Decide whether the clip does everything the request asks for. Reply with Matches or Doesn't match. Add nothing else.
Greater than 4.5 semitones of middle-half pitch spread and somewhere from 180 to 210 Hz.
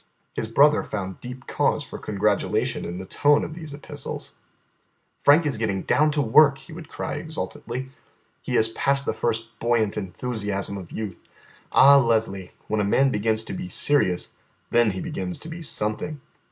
Doesn't match